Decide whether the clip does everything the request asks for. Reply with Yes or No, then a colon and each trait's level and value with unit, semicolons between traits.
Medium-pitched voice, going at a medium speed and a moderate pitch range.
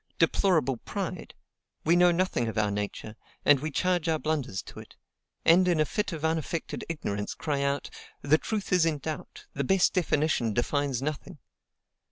Yes: medium, 155 Hz; average, 170 wpm; average, 4.0 semitones